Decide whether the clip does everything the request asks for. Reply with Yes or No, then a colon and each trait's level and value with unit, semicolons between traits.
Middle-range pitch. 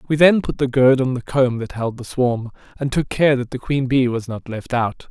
No: low, 130 Hz